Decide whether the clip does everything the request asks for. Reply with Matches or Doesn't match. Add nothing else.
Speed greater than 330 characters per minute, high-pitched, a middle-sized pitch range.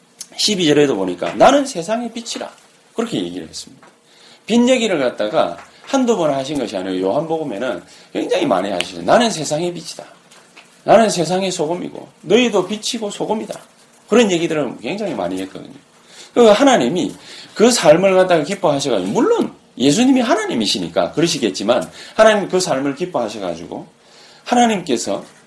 Doesn't match